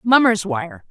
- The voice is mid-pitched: No, high, 230 Hz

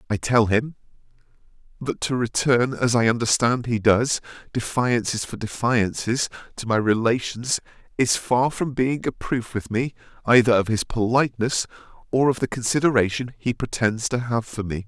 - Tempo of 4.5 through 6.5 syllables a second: Yes, 4.8 syllables/s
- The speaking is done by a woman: No, male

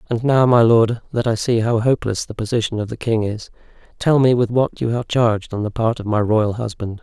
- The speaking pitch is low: Yes, low, 115 Hz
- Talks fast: Yes, fast, 250 wpm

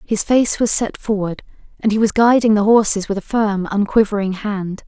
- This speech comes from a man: No, female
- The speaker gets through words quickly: No, average, 195 wpm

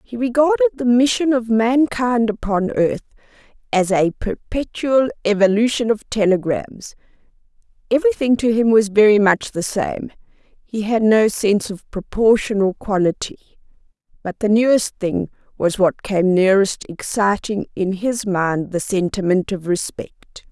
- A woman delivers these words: Yes, female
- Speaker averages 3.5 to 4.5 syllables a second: Yes, 4.3 syllables/s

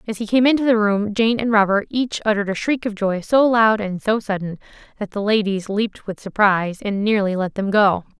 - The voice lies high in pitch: Yes, high, 210 Hz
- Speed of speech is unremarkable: No, fast, 225 wpm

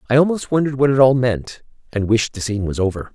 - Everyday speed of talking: No, fast, 250 wpm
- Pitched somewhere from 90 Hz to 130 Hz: Yes, low, 120 Hz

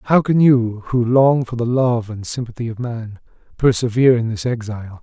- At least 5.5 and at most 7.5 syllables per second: No, 5.0 syllables/s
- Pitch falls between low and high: No, low, 120 Hz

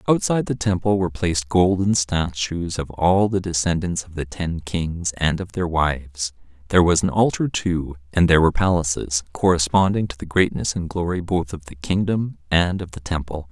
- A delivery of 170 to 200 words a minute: Yes, average, 185 wpm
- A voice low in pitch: Yes, very low, 85 Hz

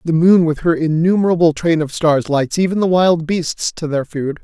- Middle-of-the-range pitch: Yes, medium, 165 Hz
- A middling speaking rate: No, fast, 215 wpm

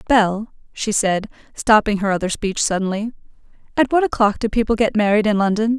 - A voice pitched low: No, high, 215 Hz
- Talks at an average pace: Yes, average, 175 wpm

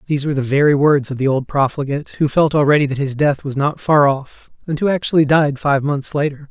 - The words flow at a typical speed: No, fast, 240 wpm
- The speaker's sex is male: Yes, male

